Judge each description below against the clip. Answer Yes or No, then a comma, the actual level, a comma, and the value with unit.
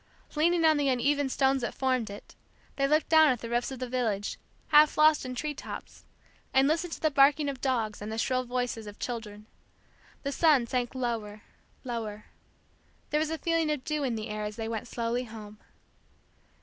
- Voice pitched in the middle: No, very high, 255 Hz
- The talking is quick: No, average, 195 wpm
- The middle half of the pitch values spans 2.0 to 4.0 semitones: No, average, 4.6 semitones